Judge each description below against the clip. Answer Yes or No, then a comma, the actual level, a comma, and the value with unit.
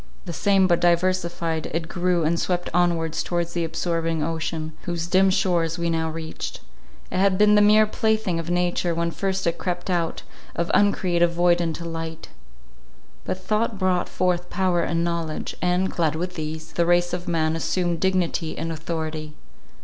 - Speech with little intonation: Yes, narrow, 1.9 semitones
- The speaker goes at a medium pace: Yes, average, 170 wpm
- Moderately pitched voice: Yes, medium, 170 Hz